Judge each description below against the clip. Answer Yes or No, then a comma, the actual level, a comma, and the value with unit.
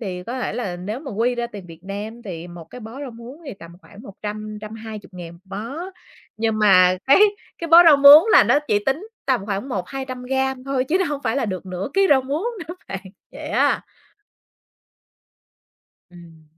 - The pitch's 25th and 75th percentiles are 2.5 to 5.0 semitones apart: No, wide, 5.6 semitones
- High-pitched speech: Yes, high, 225 Hz